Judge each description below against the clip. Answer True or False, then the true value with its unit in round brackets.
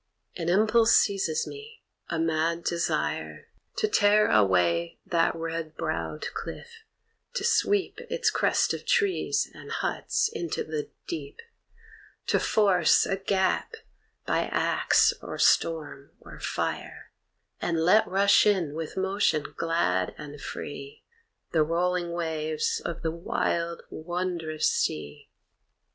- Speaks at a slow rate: True (120 wpm)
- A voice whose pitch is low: False (170 Hz)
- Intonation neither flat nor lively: True (4.4 semitones)